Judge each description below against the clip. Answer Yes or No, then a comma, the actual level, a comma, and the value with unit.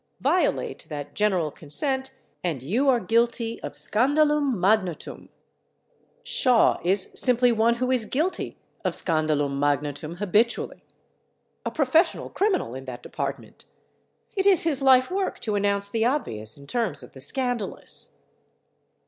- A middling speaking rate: No, slow, 130 wpm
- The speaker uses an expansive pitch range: Yes, wide, 8.3 semitones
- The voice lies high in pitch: Yes, high, 225 Hz